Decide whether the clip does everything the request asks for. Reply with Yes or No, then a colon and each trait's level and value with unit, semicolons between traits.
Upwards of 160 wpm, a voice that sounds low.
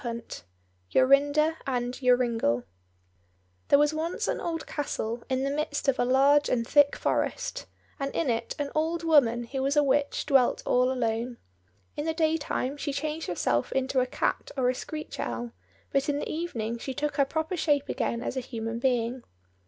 No: average, 185 wpm; very high, 275 Hz